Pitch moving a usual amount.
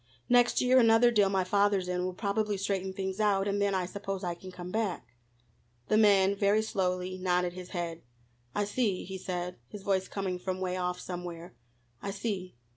No: narrow, 2.0 semitones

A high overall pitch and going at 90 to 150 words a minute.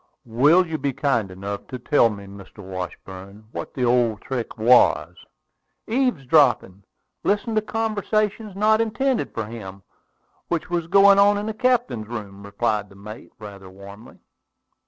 No: low, 120 Hz; average, 145 wpm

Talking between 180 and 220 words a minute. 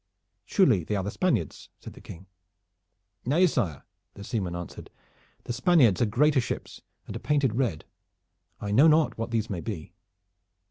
No: average, 165 wpm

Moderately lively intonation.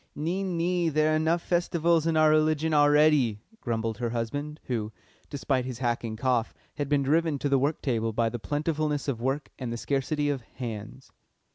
Yes: average, 4.4 semitones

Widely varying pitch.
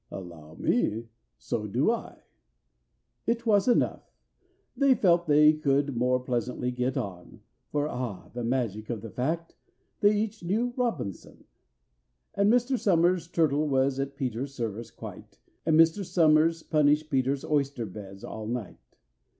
Yes: wide, 6.1 semitones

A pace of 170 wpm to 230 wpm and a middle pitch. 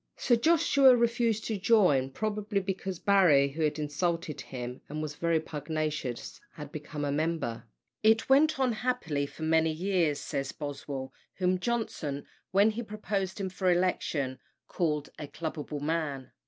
No: average, 150 wpm; medium, 165 Hz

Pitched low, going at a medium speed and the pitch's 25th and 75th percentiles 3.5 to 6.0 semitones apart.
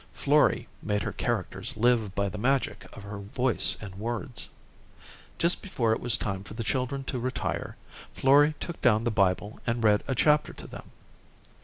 Yes: low, 115 Hz; average, 175 wpm; average, 4.2 semitones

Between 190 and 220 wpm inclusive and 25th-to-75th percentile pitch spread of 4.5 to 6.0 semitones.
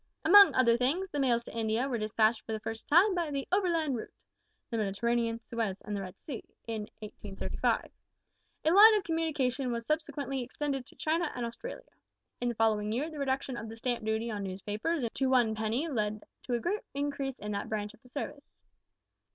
Yes: average, 195 wpm; average, 4.8 semitones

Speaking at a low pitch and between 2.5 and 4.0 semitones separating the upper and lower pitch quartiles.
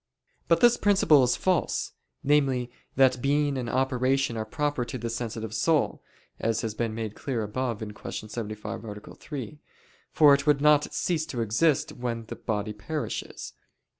No: low, 125 Hz; average, 4.5 semitones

